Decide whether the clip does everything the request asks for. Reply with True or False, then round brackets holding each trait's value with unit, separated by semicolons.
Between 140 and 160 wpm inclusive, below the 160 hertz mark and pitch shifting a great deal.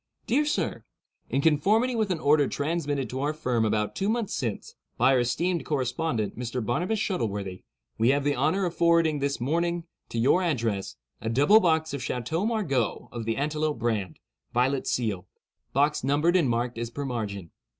False (170 wpm; 140 Hz; 6.0 semitones)